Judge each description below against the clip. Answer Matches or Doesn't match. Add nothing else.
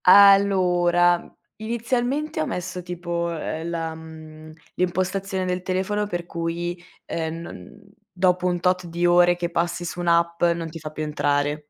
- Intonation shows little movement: Matches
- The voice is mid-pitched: Matches